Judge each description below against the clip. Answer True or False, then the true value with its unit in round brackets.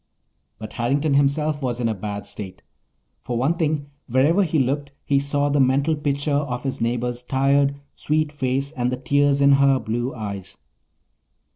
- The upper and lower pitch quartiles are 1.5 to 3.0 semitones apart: True (2.6 semitones)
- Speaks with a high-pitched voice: False (140 Hz)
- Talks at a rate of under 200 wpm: True (165 wpm)